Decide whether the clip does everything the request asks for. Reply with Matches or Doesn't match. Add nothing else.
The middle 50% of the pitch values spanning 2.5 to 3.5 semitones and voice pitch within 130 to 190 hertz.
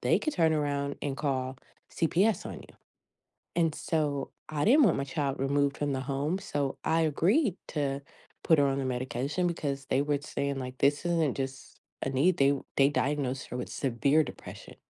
Matches